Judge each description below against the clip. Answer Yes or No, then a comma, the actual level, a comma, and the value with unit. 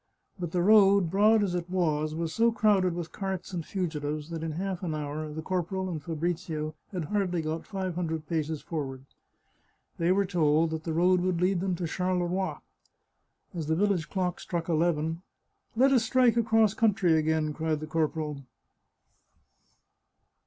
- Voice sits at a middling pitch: Yes, medium, 175 Hz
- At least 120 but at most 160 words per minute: No, average, 175 wpm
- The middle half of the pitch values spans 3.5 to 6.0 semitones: No, average, 3.1 semitones